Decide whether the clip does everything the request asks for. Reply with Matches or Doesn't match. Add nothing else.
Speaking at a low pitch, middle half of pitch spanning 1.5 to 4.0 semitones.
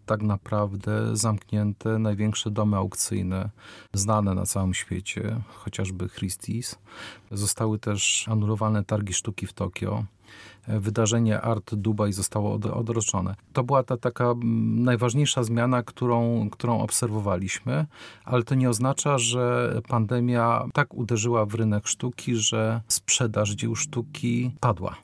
Matches